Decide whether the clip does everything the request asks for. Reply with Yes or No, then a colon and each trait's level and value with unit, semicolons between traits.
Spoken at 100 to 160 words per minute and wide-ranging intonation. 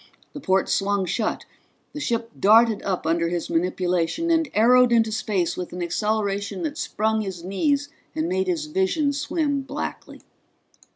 Yes: average, 155 wpm; wide, 6.0 semitones